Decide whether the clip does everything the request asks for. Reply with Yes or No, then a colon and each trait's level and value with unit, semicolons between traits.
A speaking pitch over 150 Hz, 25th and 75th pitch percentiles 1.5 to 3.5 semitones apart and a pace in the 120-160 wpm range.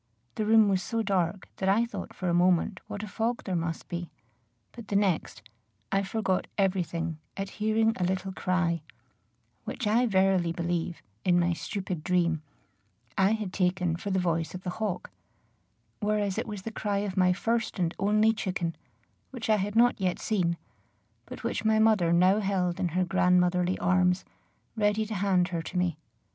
No: high, 190 Hz; average, 2.9 semitones; average, 180 wpm